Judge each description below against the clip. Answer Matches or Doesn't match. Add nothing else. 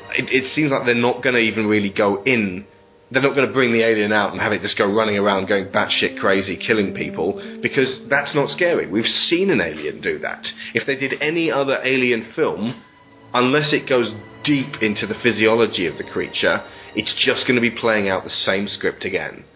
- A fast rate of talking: Matches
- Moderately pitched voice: Doesn't match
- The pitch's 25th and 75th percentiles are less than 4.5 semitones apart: Matches